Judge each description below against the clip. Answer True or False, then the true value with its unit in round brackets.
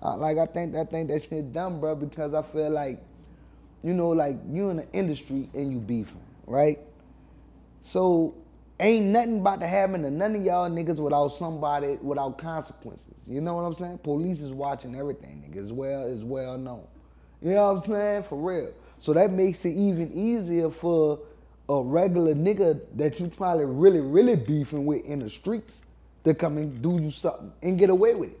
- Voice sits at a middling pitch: True (155 Hz)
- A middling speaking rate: True (195 wpm)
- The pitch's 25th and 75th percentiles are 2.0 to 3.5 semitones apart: False (4.2 semitones)